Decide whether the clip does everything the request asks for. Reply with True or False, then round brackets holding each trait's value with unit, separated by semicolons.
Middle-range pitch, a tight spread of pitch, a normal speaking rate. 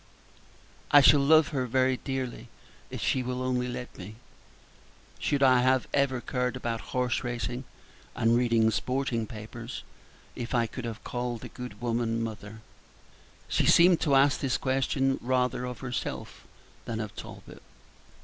False (125 Hz; 2.1 semitones; 150 wpm)